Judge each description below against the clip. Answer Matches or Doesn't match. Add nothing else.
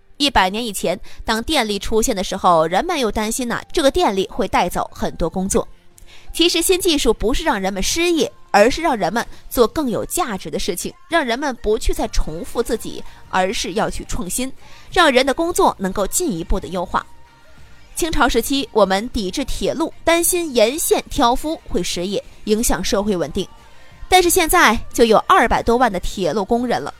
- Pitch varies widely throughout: Matches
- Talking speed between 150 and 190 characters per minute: Doesn't match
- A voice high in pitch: Matches